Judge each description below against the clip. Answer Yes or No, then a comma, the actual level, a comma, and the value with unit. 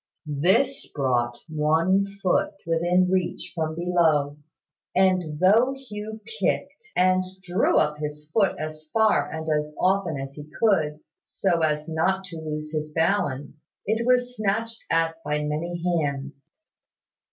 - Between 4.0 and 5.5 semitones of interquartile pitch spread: Yes, average, 4.3 semitones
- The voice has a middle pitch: Yes, medium, 165 Hz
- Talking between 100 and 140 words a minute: Yes, slow, 135 wpm